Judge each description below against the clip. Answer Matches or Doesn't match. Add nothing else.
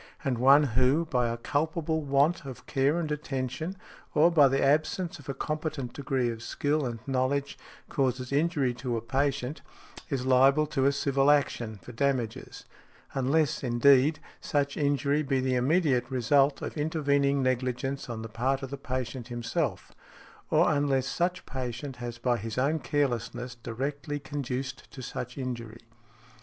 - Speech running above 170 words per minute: Doesn't match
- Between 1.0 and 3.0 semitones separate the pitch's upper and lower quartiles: Matches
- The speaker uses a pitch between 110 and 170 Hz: Matches